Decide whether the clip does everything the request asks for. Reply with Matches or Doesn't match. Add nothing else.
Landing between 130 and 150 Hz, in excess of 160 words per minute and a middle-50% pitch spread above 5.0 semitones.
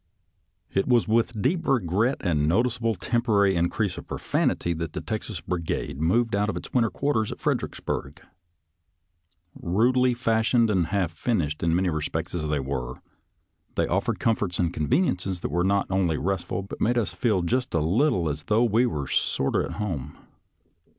Doesn't match